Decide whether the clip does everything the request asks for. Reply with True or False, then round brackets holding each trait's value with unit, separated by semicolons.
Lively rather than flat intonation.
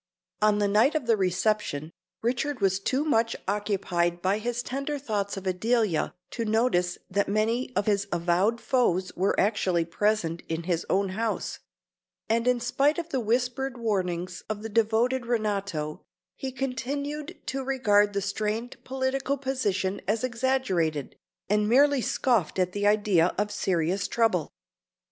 False (4.8 semitones)